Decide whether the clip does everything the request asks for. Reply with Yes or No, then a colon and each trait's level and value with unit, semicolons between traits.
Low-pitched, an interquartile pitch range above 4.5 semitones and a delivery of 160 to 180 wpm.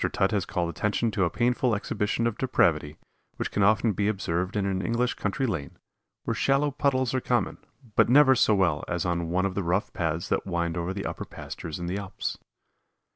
No: low, 100 Hz; average, 5.3 semitones; fast, 205 wpm